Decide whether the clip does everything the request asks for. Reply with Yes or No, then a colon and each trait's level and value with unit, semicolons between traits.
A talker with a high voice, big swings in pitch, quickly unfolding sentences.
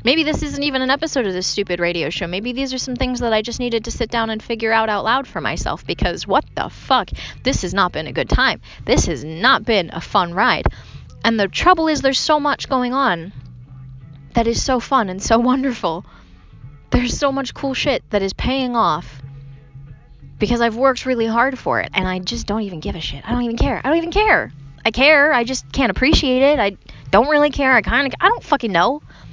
Yes: high, 230 Hz; wide, 7.0 semitones; fast, 235 wpm